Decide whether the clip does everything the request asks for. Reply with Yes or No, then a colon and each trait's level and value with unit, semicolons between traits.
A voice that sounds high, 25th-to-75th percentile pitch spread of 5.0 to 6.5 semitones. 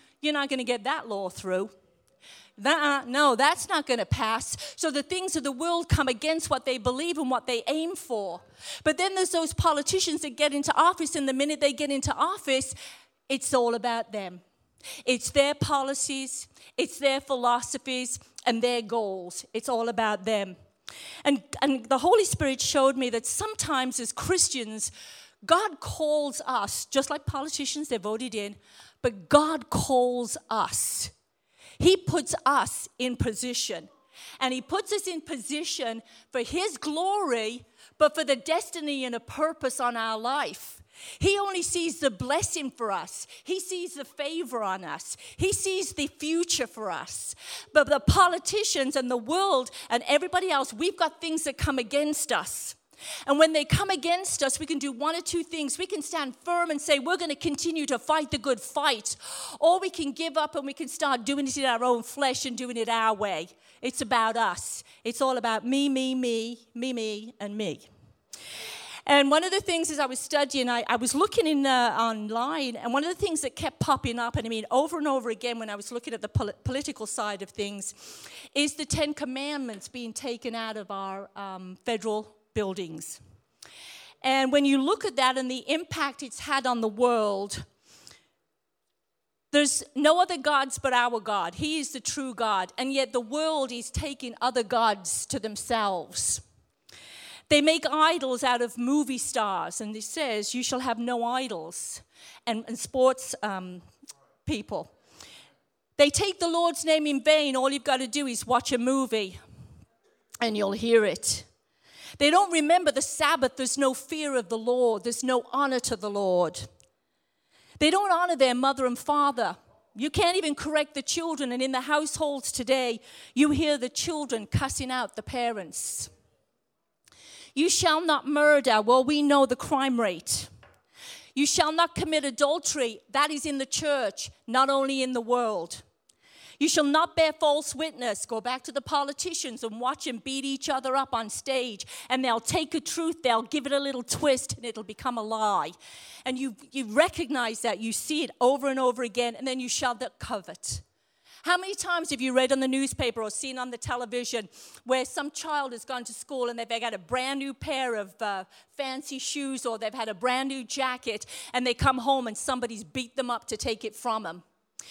No: very high, 265 Hz; average, 4.2 semitones